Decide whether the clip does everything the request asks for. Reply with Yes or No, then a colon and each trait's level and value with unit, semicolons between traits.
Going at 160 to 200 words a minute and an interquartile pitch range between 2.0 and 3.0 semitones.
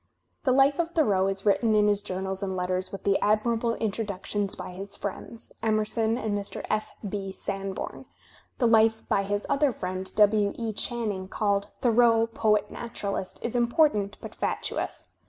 Yes: average, 165 wpm; average, 2.7 semitones